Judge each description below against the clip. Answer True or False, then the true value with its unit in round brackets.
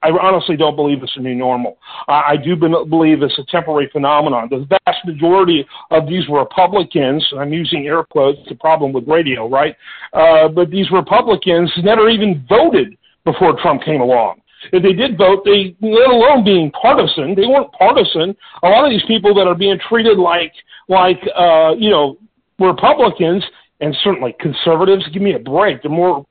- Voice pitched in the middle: True (175 Hz)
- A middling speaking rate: True (180 wpm)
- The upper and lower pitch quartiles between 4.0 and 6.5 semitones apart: True (4.3 semitones)